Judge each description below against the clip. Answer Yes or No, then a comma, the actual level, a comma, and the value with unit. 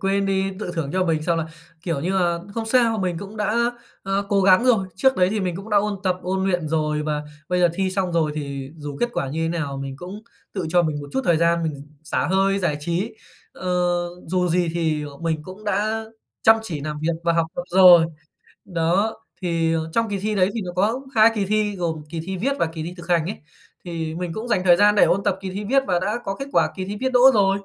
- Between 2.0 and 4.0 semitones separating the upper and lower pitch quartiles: Yes, average, 3.6 semitones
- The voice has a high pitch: No, medium, 180 Hz